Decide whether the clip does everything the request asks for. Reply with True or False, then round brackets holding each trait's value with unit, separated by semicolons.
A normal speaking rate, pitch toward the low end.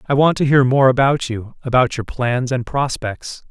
True (190 wpm; 130 Hz)